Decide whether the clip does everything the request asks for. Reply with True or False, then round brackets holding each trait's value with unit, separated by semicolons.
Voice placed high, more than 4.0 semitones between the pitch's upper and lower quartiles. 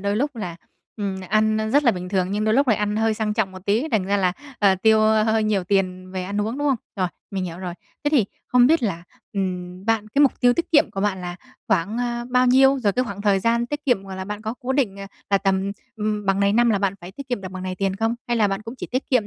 False (210 Hz; 3.6 semitones)